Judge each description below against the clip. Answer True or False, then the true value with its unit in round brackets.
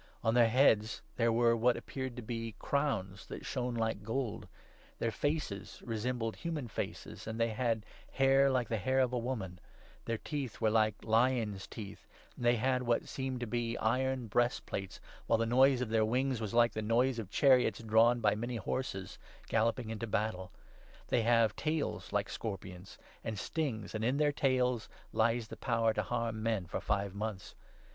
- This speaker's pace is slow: False (185 wpm)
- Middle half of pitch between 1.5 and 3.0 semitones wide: True (2.6 semitones)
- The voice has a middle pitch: False (115 Hz)